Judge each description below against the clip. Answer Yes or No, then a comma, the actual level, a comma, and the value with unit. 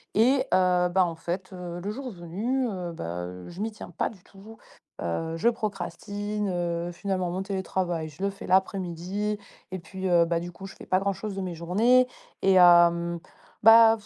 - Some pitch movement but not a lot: Yes, average, 3.0 semitones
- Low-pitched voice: No, medium, 185 Hz